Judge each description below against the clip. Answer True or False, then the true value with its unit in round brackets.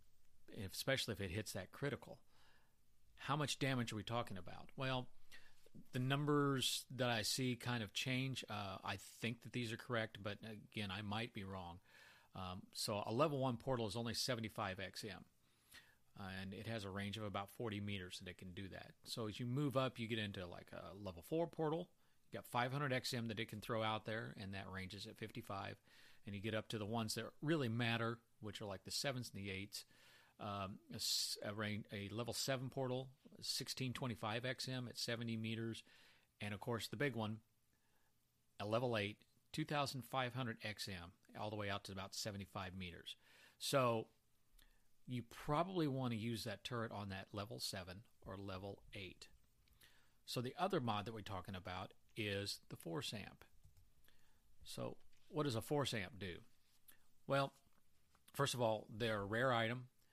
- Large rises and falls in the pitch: False (4.0 semitones)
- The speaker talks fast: False (180 wpm)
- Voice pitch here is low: True (115 Hz)